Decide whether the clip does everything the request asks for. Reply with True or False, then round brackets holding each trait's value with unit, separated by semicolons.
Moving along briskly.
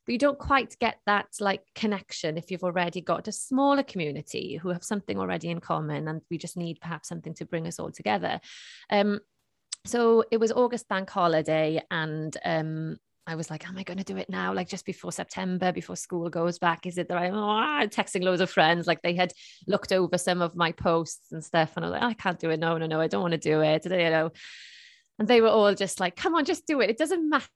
True (245 wpm)